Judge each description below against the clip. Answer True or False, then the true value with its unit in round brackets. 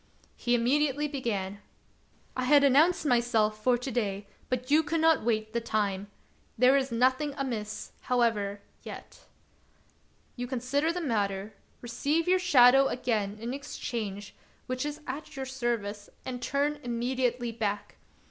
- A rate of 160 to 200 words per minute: False (145 wpm)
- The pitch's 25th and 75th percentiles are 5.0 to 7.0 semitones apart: False (4.3 semitones)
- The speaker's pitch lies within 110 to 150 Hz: False (245 Hz)